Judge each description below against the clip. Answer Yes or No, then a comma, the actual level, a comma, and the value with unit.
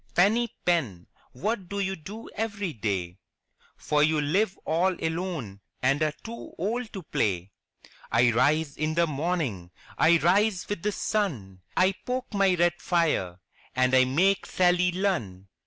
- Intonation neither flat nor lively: No, wide, 7.1 semitones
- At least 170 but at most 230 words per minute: No, average, 155 wpm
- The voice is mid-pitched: Yes, medium, 170 Hz